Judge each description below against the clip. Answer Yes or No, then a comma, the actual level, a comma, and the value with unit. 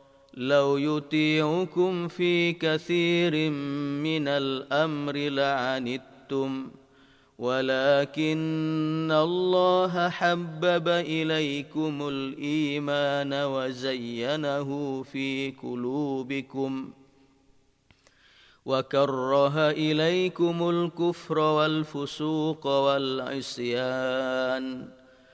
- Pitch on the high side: No, medium, 140 Hz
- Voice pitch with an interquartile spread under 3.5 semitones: Yes, average, 2.7 semitones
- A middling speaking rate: No, slow, 45 wpm